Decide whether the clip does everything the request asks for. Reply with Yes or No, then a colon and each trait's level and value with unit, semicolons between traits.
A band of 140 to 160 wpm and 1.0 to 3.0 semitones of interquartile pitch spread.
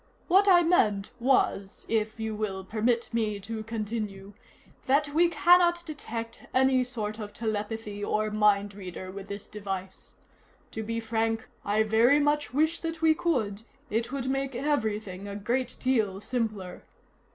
No: average, 150 wpm; average, 4.3 semitones